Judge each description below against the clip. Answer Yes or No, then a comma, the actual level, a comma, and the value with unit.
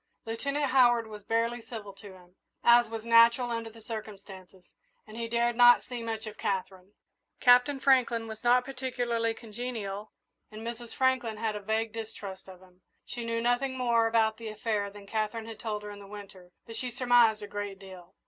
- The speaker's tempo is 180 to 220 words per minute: Yes, average, 185 wpm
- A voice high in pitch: Yes, high, 225 Hz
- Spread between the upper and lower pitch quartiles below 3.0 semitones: Yes, narrow, 2.5 semitones